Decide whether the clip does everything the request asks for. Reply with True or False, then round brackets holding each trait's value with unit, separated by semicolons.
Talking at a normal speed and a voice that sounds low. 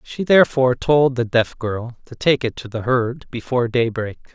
True (195 wpm; 125 Hz)